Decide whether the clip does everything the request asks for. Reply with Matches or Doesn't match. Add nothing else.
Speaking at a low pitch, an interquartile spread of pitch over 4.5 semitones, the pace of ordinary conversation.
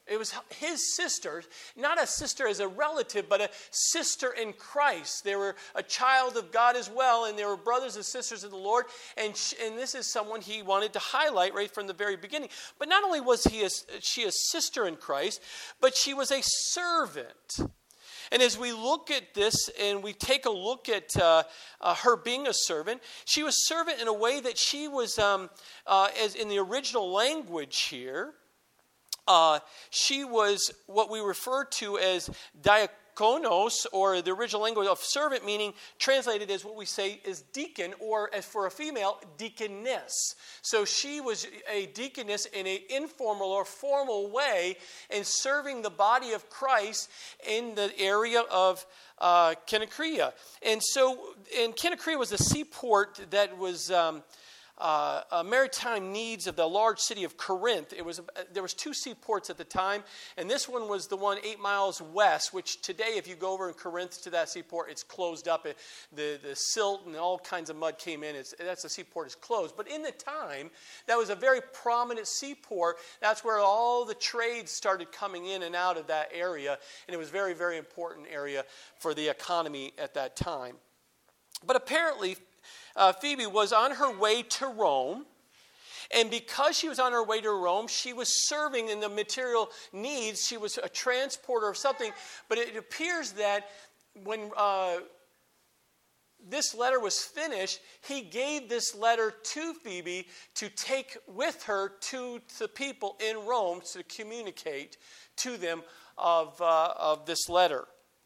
Doesn't match